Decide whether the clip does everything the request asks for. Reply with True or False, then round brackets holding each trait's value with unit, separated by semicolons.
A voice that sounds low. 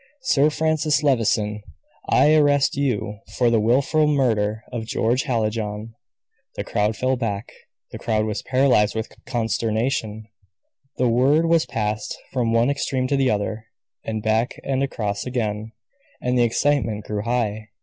True (115 Hz)